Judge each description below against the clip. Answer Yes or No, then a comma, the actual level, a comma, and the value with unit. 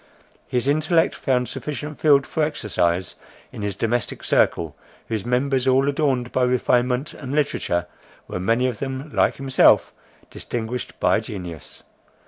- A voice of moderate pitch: No, low, 125 Hz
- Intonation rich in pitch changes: No, average, 3.9 semitones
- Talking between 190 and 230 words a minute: No, slow, 135 wpm